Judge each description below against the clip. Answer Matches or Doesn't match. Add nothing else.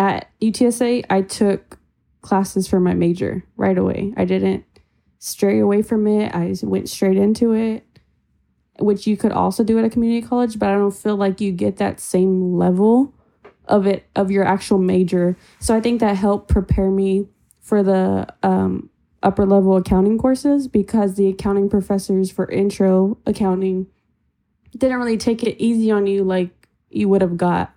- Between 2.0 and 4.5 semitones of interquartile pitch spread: Matches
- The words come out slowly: Doesn't match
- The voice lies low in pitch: Doesn't match